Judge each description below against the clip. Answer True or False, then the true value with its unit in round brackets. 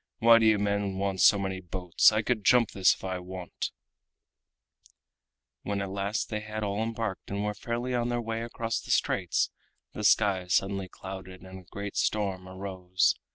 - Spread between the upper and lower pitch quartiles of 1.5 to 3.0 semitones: True (2.6 semitones)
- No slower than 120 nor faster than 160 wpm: False (180 wpm)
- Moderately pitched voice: False (100 Hz)